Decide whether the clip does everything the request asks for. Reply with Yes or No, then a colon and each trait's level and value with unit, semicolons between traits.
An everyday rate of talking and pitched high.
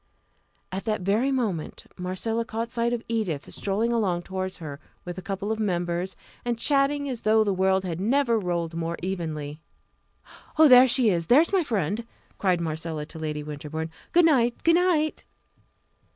Yes: average, 170 wpm; high, 195 Hz